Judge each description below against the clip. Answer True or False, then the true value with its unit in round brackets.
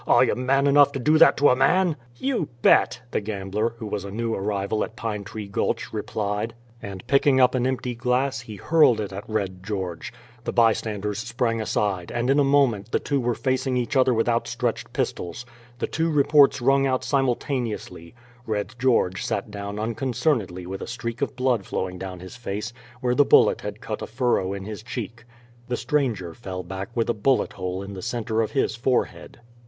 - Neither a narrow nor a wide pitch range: True (4.2 semitones)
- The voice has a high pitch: False (115 Hz)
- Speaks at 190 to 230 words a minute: True (200 wpm)